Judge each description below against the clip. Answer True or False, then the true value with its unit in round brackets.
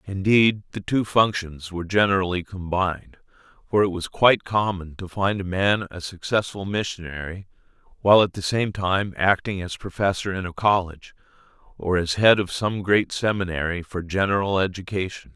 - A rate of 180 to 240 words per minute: False (155 wpm)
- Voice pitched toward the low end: True (95 Hz)